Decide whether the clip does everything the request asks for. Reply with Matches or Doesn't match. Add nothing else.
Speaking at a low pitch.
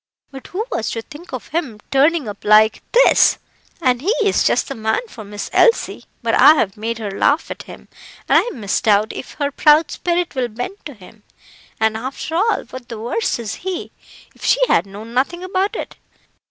Doesn't match